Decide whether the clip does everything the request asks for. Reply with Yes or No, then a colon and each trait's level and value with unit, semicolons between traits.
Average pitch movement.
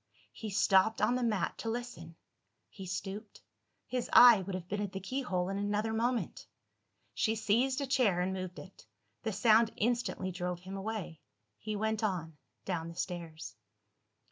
Yes: average, 3.4 semitones